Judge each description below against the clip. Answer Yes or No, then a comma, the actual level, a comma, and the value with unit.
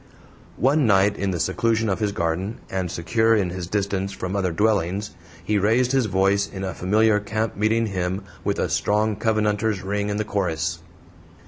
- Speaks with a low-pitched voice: Yes, low, 100 Hz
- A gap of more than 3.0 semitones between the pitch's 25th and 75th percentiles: No, narrow, 2.4 semitones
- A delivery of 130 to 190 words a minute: Yes, average, 180 wpm